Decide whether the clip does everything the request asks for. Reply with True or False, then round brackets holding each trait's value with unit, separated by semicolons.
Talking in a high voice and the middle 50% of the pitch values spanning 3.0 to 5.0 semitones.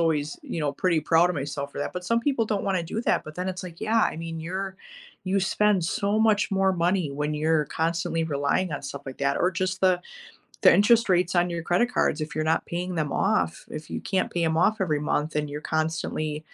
False (170 Hz; 3.5 semitones)